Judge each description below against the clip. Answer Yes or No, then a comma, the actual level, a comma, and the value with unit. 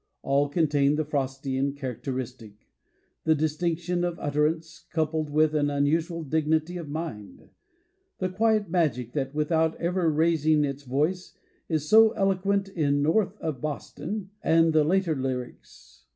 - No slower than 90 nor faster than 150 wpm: Yes, slow, 135 wpm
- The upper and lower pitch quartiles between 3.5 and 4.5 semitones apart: No, average, 3.1 semitones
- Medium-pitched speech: Yes, medium, 155 Hz